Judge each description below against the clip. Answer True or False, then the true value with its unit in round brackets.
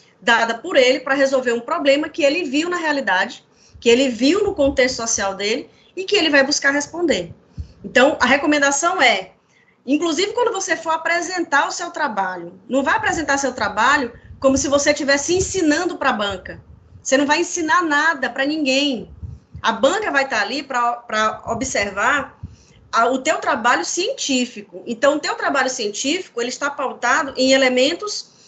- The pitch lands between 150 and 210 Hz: False (280 Hz)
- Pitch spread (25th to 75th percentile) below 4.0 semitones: False (4.5 semitones)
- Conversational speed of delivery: True (165 wpm)